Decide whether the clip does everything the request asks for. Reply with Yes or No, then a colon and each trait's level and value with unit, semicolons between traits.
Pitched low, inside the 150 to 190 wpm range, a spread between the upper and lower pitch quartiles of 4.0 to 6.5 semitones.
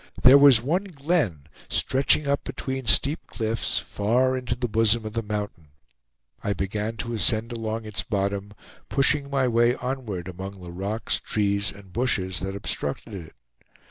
Yes: low, 110 Hz; average, 155 wpm; average, 4.4 semitones